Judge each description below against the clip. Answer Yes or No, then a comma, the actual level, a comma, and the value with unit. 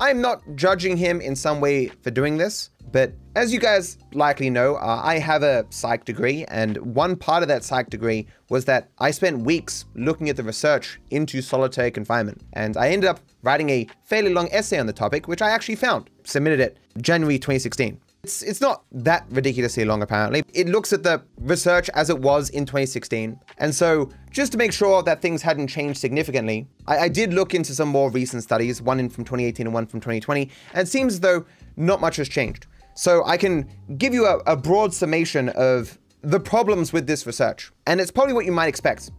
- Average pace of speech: No, fast, 210 wpm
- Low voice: No, medium, 150 Hz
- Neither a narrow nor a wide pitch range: No, wide, 6.0 semitones